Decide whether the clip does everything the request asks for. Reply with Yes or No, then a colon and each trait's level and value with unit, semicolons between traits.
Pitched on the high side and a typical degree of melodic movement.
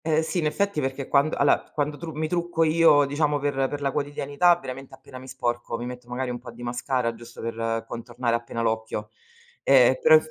No: low, 135 Hz; average, 4.1 semitones